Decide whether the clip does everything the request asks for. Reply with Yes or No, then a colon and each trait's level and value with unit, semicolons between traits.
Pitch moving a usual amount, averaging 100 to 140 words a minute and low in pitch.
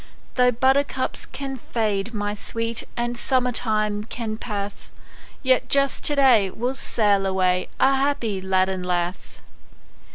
No: average, 4.5 semitones; slow, 135 wpm; high, 225 Hz